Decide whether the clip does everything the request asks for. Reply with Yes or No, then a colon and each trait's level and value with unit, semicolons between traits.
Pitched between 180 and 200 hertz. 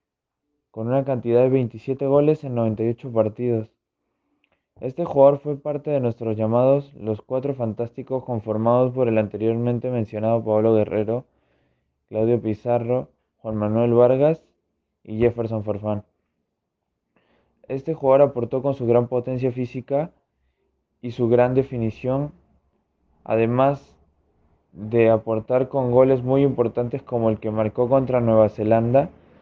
No: low, 120 Hz